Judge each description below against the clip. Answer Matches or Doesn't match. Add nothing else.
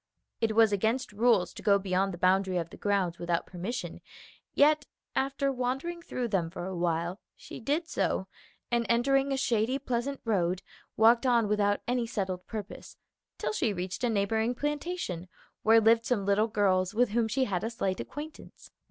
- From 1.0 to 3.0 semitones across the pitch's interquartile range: Doesn't match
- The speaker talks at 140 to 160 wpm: Doesn't match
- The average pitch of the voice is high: Matches